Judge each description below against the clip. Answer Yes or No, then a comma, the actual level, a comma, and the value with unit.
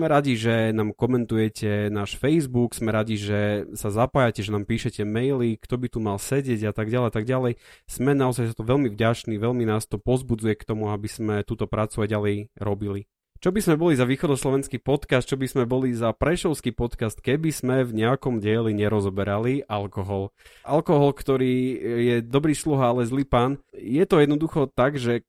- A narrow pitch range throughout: No, average, 3.8 semitones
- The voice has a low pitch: Yes, low, 120 Hz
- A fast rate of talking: Yes, fast, 190 wpm